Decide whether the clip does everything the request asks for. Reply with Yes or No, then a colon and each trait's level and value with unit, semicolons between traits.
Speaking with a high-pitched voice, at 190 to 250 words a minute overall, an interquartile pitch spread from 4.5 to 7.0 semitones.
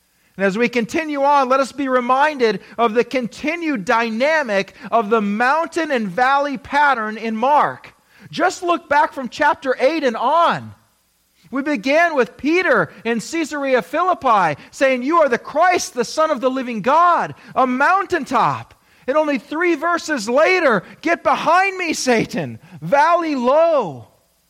No: very high, 275 Hz; average, 145 wpm; average, 5.1 semitones